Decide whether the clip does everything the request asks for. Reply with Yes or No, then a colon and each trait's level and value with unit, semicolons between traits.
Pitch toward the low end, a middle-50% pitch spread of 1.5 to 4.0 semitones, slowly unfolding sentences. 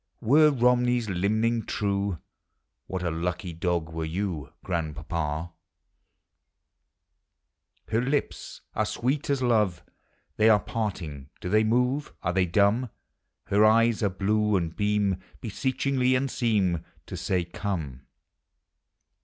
No: low, 100 Hz; average, 5.1 semitones; slow, 125 wpm